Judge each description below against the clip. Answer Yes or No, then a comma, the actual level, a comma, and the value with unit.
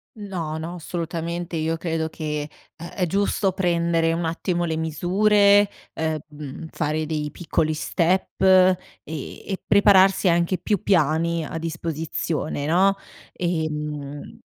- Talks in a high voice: No, medium, 165 Hz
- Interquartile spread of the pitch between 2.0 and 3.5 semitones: Yes, average, 2.7 semitones